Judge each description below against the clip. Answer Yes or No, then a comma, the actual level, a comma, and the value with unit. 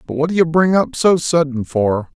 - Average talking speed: No, fast, 245 wpm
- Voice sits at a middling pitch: Yes, medium, 155 Hz